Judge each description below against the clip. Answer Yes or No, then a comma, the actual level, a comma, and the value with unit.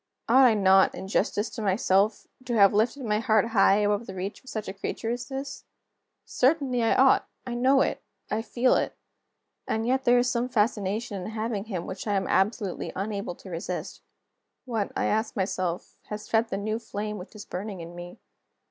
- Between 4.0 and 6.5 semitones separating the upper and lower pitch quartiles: No, average, 3.4 semitones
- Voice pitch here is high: Yes, high, 215 Hz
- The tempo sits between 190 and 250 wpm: Yes, average, 195 wpm